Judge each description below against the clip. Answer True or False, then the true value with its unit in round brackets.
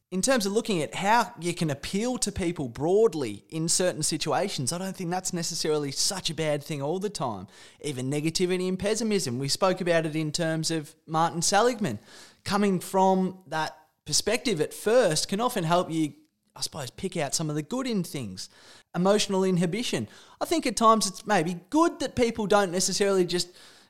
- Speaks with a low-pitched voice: False (185 Hz)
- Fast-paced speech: False (185 wpm)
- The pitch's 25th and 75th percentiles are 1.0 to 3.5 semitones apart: False (4.3 semitones)